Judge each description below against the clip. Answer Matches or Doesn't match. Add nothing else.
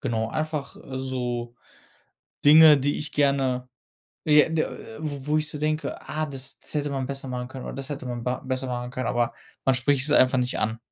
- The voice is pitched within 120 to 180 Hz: Matches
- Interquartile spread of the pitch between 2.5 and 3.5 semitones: Matches